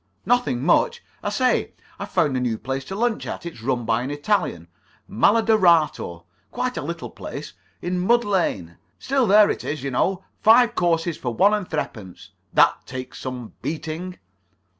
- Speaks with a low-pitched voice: No, medium, 165 Hz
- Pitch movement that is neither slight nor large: No, wide, 8.5 semitones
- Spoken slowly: No, average, 165 wpm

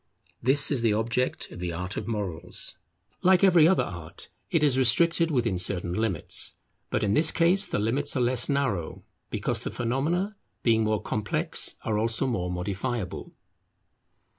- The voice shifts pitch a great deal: Yes, wide, 6.2 semitones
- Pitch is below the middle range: Yes, low, 115 Hz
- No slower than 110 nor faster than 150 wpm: No, average, 160 wpm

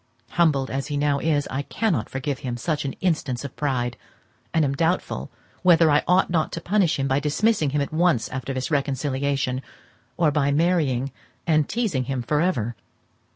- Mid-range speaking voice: Yes, medium, 145 Hz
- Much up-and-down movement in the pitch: No, average, 3.5 semitones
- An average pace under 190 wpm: Yes, average, 180 wpm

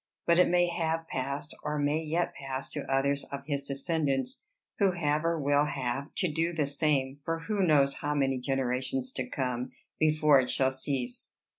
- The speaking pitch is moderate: Yes, medium, 145 Hz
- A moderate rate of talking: Yes, average, 180 wpm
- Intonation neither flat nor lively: Yes, average, 3.2 semitones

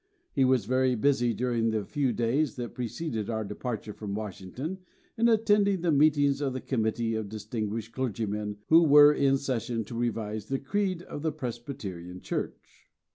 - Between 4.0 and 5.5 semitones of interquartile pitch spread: Yes, average, 4.7 semitones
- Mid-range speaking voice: No, low, 125 Hz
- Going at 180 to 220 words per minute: No, average, 165 wpm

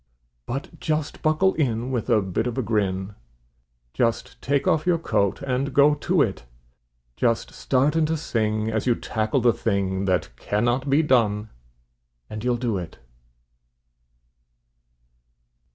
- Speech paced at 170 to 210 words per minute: No, average, 140 wpm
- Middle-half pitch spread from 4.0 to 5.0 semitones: Yes, average, 4.7 semitones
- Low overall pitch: Yes, low, 120 Hz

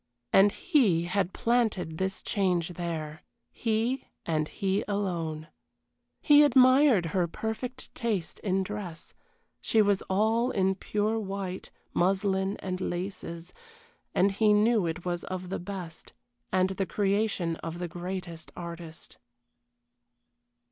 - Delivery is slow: Yes, slow, 120 wpm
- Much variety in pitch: No, average, 3.4 semitones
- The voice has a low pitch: No, high, 190 Hz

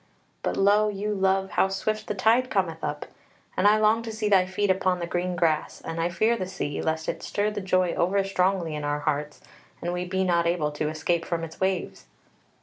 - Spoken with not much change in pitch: No, average, 3.5 semitones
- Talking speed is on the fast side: Yes, fast, 220 wpm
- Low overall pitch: No, medium, 185 Hz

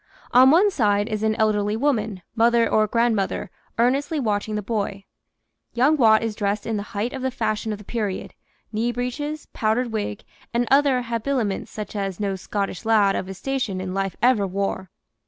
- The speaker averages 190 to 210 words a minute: No, average, 180 wpm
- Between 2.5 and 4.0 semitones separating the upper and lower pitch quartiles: Yes, average, 3.2 semitones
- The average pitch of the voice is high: Yes, high, 220 Hz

